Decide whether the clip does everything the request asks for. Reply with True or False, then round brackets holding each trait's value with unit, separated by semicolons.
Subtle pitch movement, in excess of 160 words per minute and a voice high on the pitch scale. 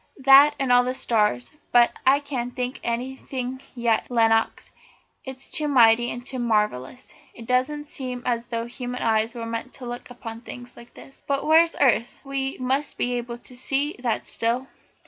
True (2.2 semitones; 185 wpm; 245 Hz)